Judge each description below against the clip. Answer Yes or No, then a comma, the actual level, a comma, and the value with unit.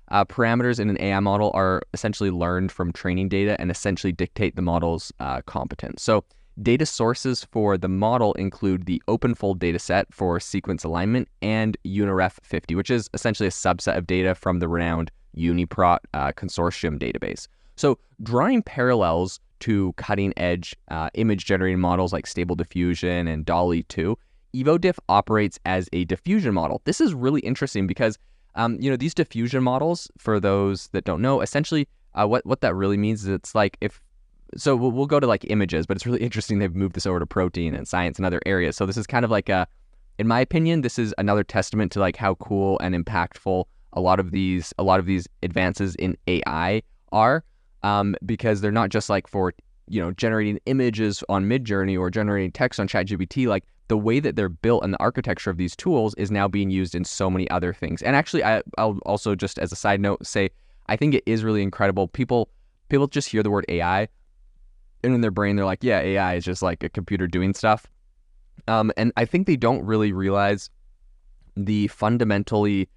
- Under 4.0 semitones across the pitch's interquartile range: Yes, average, 3.4 semitones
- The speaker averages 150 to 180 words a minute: No, average, 195 wpm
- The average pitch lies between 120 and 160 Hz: No, low, 100 Hz